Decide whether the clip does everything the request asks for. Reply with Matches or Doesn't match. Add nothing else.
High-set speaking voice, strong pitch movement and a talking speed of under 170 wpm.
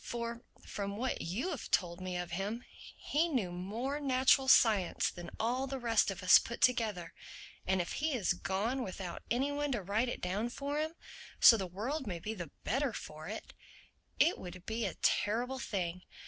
Doesn't match